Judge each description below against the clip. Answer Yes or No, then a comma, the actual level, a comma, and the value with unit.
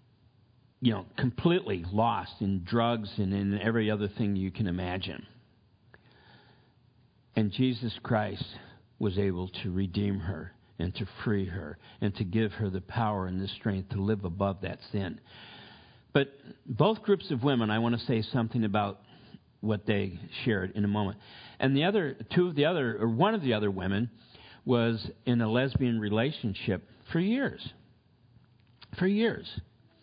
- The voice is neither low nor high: No, low, 110 Hz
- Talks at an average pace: Yes, average, 160 wpm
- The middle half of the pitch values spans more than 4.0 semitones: No, average, 3.6 semitones